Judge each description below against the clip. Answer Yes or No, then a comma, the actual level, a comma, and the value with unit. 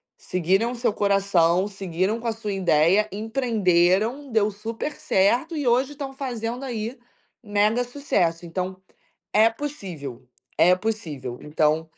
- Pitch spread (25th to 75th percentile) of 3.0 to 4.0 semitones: No, average, 4.8 semitones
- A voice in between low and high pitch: No, high, 210 Hz